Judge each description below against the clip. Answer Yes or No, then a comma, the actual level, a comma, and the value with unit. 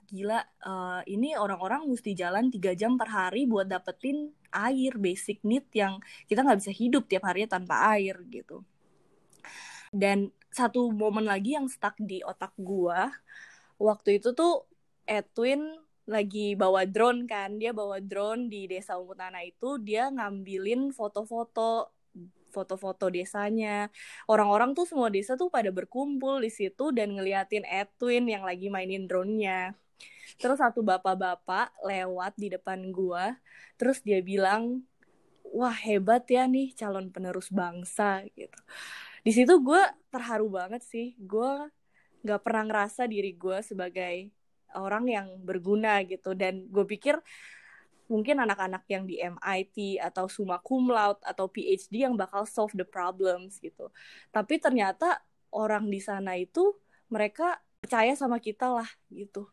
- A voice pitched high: Yes, high, 210 Hz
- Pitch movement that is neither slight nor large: Yes, average, 4.1 semitones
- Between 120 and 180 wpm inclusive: Yes, fast, 140 wpm